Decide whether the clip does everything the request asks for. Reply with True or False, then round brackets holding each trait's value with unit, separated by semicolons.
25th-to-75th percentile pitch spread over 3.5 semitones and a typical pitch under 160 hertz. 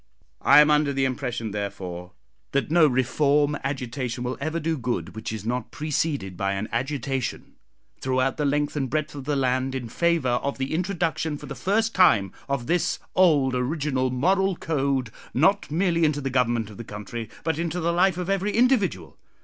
True (4.7 semitones; 140 Hz)